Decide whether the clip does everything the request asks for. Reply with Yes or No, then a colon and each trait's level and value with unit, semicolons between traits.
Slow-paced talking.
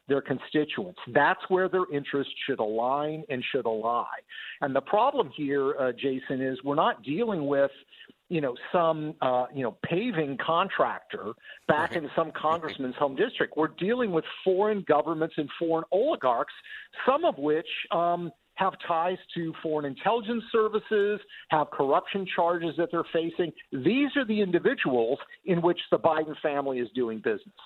No: average, 155 wpm